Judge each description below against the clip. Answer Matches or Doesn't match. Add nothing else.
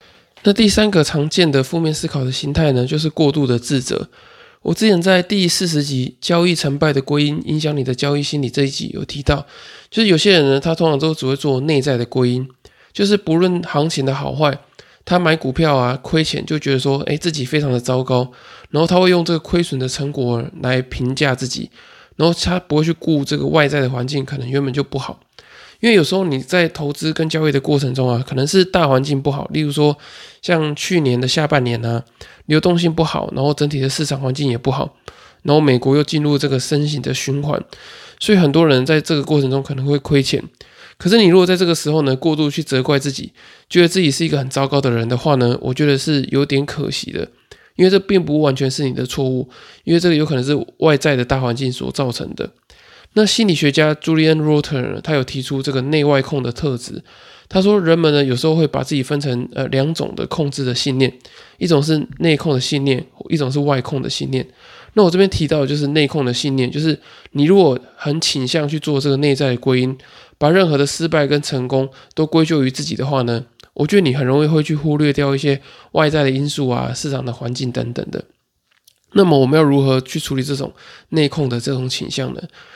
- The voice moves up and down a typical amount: Matches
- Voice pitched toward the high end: Doesn't match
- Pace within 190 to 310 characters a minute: Doesn't match